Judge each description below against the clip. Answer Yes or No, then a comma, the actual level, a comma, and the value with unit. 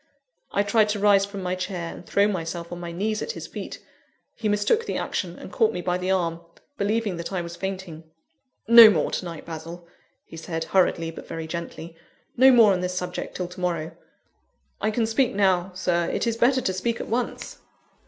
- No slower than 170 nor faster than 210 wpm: Yes, fast, 205 wpm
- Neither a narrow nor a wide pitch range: Yes, average, 3.6 semitones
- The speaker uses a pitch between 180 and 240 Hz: Yes, medium, 185 Hz